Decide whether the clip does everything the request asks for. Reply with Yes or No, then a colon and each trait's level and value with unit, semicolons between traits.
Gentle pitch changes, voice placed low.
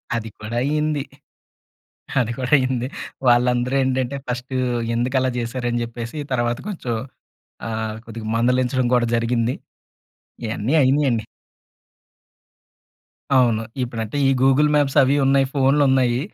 Yes: narrow, 2.2 semitones; low, 125 Hz